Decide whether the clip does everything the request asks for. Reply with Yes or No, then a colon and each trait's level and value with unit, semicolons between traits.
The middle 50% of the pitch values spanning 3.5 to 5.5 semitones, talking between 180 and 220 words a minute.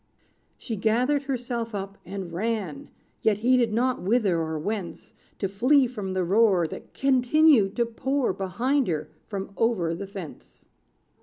No: average, 4.6 semitones; average, 145 wpm